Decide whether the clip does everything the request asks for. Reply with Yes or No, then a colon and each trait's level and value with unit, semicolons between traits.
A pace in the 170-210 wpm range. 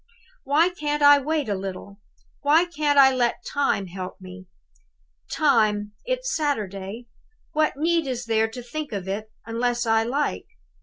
No: average, 150 wpm